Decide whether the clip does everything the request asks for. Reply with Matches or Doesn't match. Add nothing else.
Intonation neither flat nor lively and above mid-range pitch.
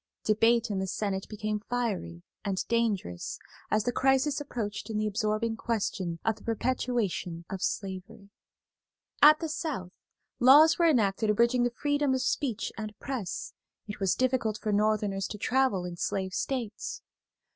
Matches